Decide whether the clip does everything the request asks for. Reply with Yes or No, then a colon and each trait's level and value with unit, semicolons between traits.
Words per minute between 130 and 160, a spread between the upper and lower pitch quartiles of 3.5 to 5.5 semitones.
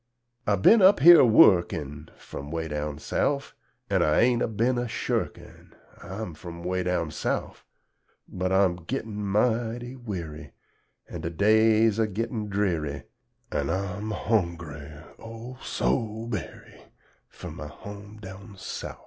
Yes: average, 140 wpm; average, 5.0 semitones